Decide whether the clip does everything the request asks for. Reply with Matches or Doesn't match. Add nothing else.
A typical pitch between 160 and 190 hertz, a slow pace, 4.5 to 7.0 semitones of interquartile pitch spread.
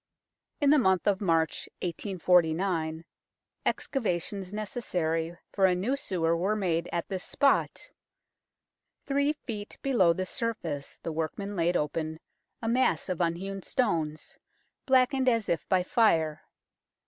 Matches